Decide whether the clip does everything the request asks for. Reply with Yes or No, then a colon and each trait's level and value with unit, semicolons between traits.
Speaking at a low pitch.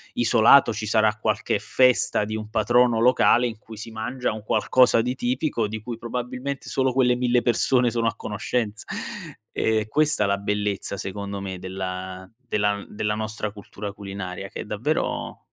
Yes: low, 110 Hz